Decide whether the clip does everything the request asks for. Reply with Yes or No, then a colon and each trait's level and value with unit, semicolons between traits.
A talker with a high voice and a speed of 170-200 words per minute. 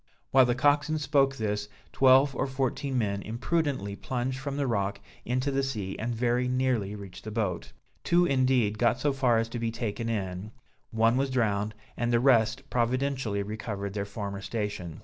No: low, 120 Hz; average, 175 wpm